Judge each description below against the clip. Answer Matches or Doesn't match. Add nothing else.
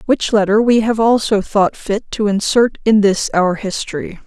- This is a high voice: Matches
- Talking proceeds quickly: Doesn't match